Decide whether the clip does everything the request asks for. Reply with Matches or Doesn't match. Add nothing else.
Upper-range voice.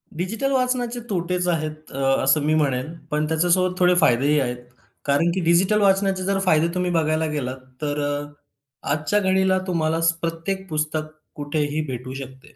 Doesn't match